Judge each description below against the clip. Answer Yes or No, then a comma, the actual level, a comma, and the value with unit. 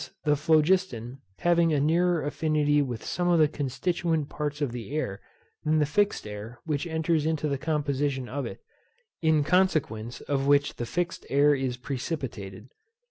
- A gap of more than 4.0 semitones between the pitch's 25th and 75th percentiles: No, average, 3.3 semitones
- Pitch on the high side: No, medium, 145 Hz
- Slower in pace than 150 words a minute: No, average, 160 wpm